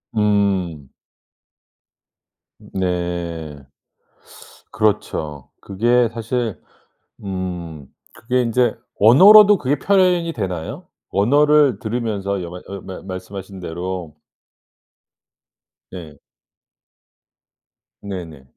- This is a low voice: Yes, low, 100 Hz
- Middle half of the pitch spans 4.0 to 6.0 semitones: Yes, wide, 5.4 semitones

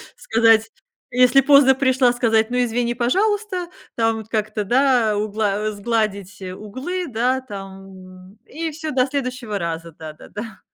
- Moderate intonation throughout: Yes, average, 4.1 semitones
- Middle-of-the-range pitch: No, high, 225 Hz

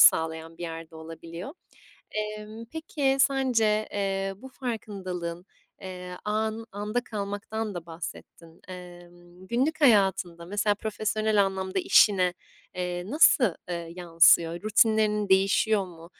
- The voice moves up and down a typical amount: Yes, average, 3.8 semitones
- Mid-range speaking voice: No, high, 195 Hz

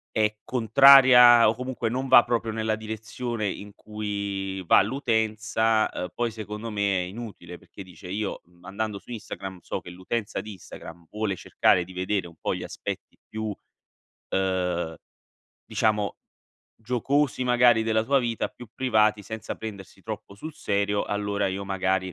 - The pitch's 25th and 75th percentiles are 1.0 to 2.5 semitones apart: No, average, 2.9 semitones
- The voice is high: No, low, 110 Hz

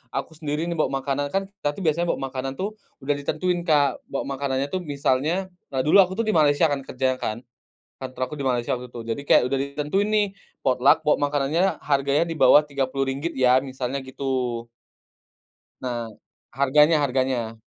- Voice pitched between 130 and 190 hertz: Yes, medium, 140 Hz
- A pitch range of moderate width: Yes, average, 3.0 semitones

